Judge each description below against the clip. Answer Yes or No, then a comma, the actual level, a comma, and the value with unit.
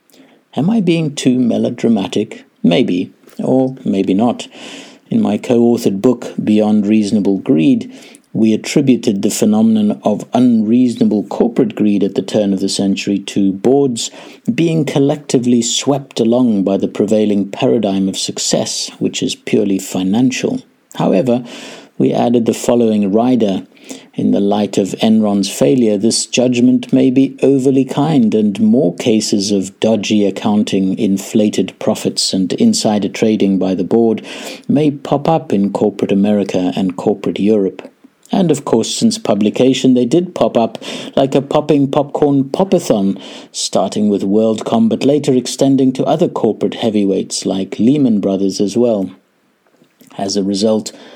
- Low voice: Yes, low, 120 Hz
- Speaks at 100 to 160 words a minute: Yes, average, 140 wpm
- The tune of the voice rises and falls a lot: Yes, wide, 6.0 semitones